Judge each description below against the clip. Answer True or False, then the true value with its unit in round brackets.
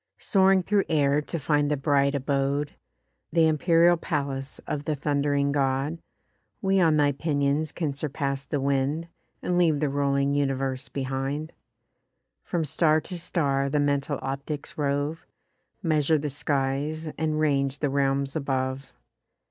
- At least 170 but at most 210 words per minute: False (140 wpm)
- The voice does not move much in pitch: True (2.2 semitones)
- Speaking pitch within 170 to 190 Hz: False (145 Hz)